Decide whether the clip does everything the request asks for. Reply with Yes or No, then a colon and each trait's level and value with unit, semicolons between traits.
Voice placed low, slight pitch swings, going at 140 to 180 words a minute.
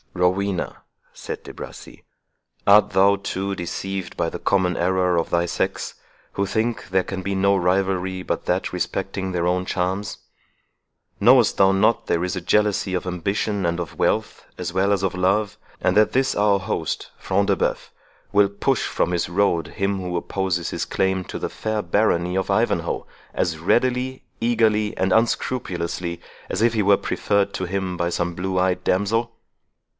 Yes: very low, 95 Hz; narrow, 2.2 semitones; average, 170 wpm